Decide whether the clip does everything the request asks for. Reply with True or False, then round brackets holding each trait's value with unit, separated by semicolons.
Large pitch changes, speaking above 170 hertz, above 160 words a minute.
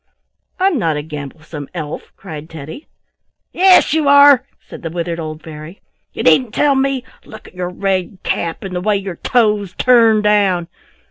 True (6.9 semitones; 190 Hz; 170 wpm)